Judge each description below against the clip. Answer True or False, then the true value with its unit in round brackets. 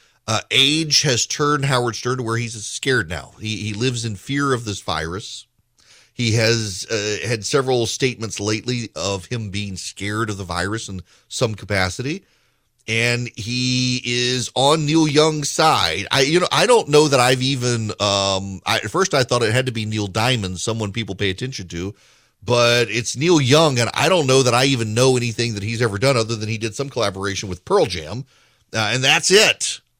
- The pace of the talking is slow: False (200 wpm)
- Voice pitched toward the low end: True (120 Hz)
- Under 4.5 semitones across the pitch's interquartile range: True (3.4 semitones)